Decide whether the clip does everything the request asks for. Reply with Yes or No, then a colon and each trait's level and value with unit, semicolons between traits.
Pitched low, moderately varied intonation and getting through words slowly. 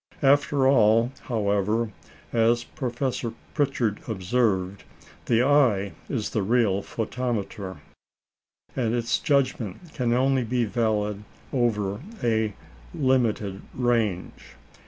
Yes: low, 115 Hz; average, 3.3 semitones; slow, 95 wpm